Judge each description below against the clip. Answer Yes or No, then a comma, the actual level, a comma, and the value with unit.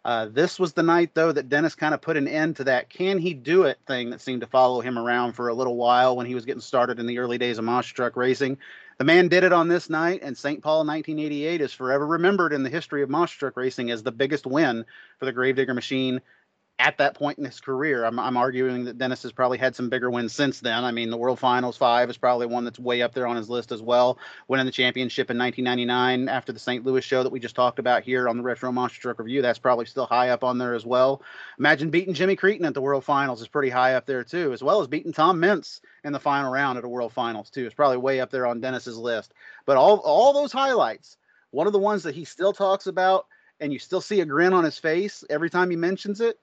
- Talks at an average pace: No, fast, 265 wpm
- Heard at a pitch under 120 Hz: No, low, 130 Hz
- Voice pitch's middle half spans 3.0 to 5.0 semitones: Yes, average, 4.0 semitones